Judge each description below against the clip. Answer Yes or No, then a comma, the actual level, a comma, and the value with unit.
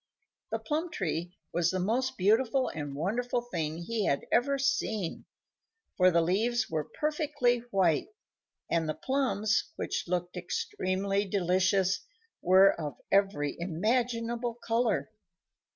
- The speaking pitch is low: No, high, 195 Hz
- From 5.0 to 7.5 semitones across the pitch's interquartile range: Yes, wide, 5.5 semitones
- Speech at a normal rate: No, slow, 120 wpm